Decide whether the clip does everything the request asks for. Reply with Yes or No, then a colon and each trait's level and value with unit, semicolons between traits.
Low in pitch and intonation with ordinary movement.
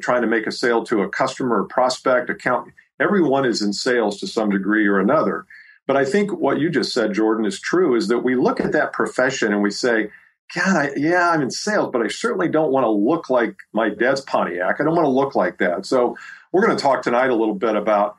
Yes: low, 110 Hz; average, 3.6 semitones